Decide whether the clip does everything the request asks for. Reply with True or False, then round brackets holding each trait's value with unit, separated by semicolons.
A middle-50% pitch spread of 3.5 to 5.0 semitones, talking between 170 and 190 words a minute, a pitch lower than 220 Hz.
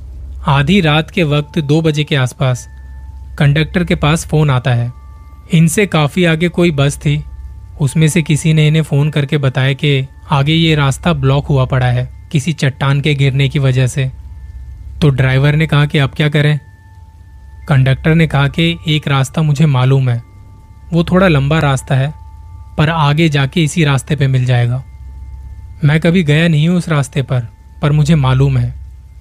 True (4.4 semitones; 175 wpm; 140 Hz)